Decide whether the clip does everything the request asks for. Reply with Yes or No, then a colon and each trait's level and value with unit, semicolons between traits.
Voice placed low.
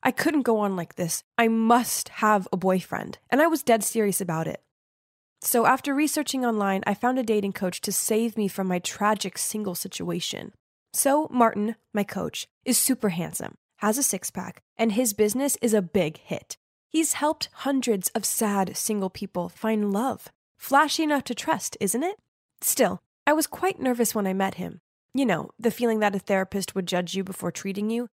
No: high, 215 Hz